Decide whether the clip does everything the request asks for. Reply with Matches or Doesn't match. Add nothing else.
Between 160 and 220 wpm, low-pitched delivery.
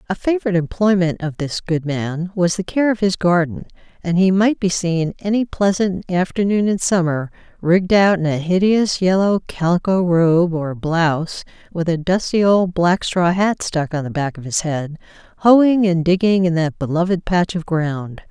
Doesn't match